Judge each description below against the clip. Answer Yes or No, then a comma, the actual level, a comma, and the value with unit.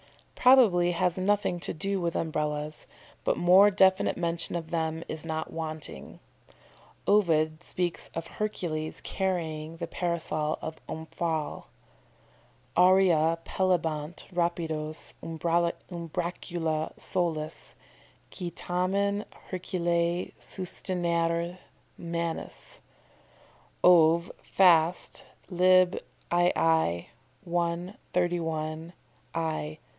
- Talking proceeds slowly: Yes, slow, 85 wpm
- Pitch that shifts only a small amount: Yes, narrow, 2.0 semitones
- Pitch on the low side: No, medium, 170 Hz